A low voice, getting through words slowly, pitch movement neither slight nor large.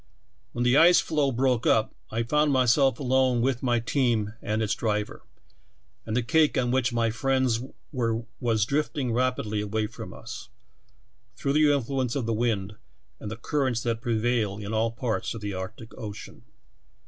No: low, 120 Hz; average, 170 wpm; average, 3.1 semitones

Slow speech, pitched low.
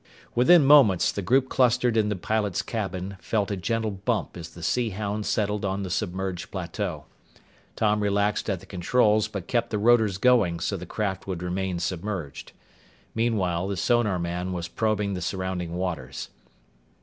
No: average, 160 wpm; low, 100 Hz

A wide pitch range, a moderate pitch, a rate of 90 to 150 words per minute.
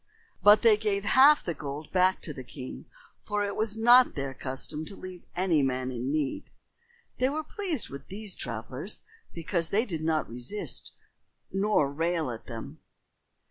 No: wide, 7.2 semitones; medium, 175 Hz; average, 165 wpm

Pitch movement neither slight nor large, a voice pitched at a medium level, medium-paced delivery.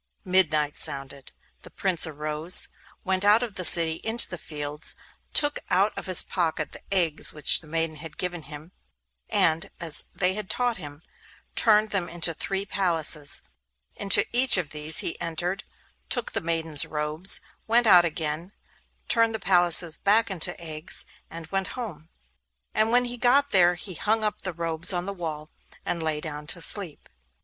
Yes: average, 3.9 semitones; medium, 175 Hz; average, 170 wpm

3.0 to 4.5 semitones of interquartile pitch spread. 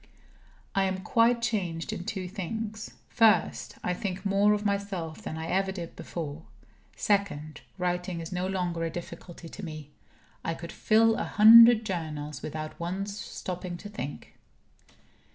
Yes: average, 3.7 semitones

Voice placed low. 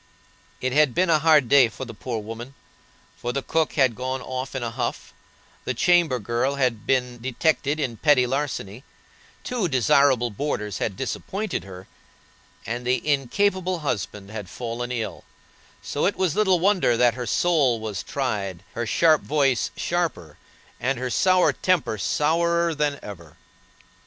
Yes: low, 130 Hz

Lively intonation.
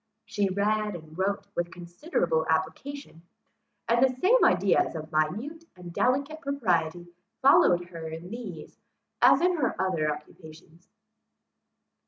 Yes: wide, 7.7 semitones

